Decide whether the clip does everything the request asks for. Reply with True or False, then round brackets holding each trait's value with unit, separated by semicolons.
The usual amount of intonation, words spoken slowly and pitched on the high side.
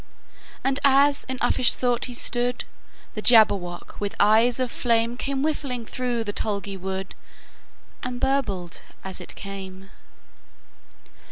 True (4.2 semitones; 110 wpm; 235 Hz)